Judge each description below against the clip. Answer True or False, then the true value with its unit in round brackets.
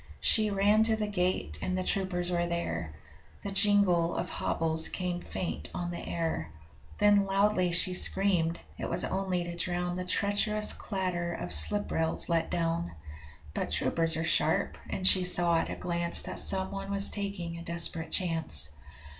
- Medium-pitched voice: True (180 Hz)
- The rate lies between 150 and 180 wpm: True (165 wpm)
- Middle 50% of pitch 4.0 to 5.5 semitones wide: False (2.7 semitones)